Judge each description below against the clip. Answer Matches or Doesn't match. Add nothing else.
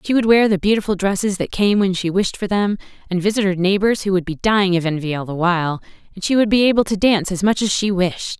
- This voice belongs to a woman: Matches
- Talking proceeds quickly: Matches